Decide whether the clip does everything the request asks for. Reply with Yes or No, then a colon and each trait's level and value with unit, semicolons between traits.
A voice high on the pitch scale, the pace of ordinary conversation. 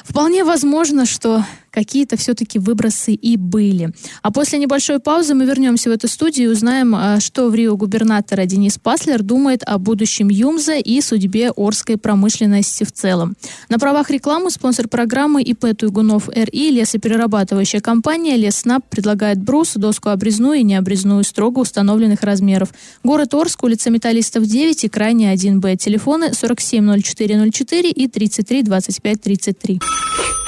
Yes: high, 225 Hz; average, 130 wpm